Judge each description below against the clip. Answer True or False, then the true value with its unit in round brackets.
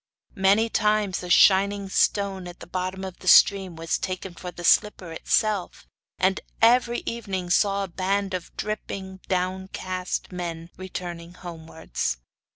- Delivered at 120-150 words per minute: True (140 wpm)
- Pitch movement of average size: False (2.0 semitones)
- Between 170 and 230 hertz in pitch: True (190 Hz)